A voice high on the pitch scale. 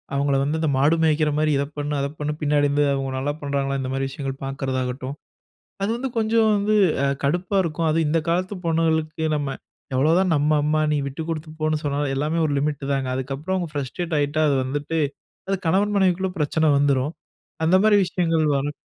No: medium, 150 Hz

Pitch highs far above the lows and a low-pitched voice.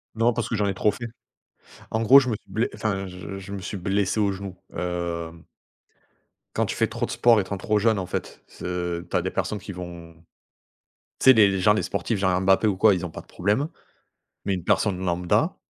No: average, 2.9 semitones; very low, 95 Hz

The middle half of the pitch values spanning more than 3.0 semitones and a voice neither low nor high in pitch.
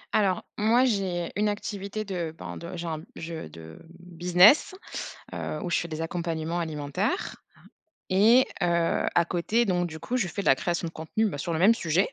Yes: average, 3.8 semitones; medium, 175 Hz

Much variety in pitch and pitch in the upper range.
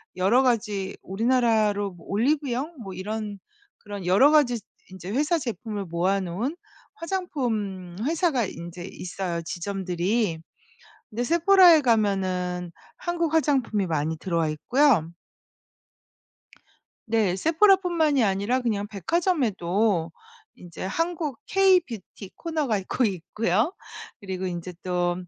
Yes: wide, 7.4 semitones; high, 210 Hz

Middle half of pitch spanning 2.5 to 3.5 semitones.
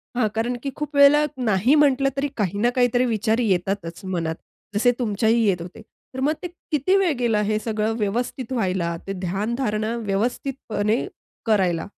No: average, 4.1 semitones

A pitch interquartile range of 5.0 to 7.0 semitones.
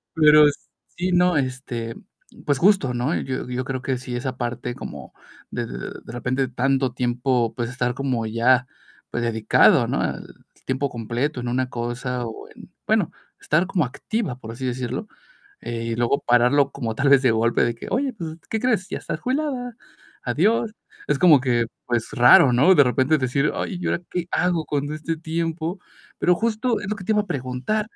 Yes: wide, 5.5 semitones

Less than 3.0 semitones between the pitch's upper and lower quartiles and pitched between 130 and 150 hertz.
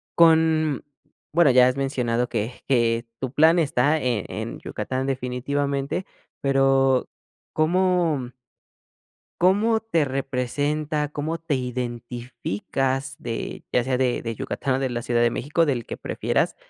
No: average, 3.6 semitones; low, 135 Hz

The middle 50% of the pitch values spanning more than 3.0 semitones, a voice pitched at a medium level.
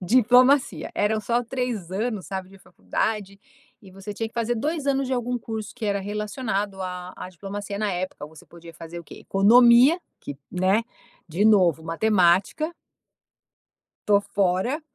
No: average, 4.2 semitones; high, 205 Hz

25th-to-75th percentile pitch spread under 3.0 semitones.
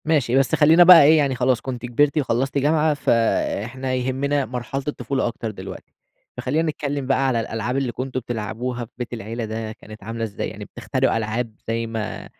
No: average, 3.4 semitones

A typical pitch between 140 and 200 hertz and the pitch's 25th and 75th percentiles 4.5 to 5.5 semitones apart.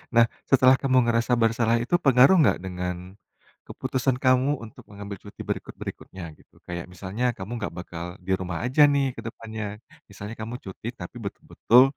No: low, 115 Hz; average, 4.9 semitones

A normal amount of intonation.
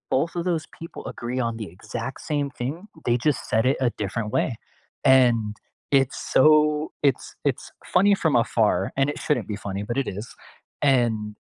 Yes: average, 4.6 semitones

